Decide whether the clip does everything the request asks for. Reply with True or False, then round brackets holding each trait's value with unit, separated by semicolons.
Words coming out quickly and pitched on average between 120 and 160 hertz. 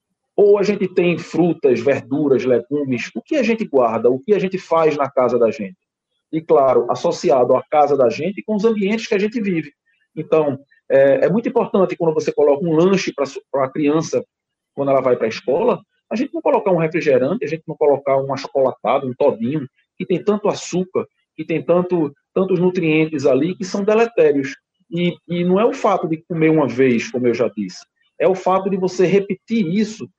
False (205 wpm; 170 Hz)